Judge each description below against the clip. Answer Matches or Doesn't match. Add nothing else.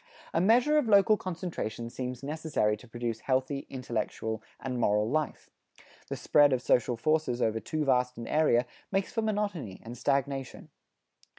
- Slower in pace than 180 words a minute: Matches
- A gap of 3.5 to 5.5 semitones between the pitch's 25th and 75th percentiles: Matches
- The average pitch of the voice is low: Matches